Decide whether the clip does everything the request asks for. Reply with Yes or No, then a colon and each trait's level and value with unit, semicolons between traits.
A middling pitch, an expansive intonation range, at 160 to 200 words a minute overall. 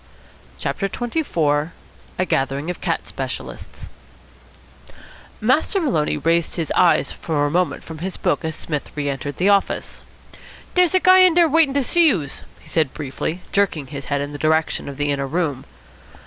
Yes: medium, 165 Hz; wide, 7.8 semitones; average, 170 wpm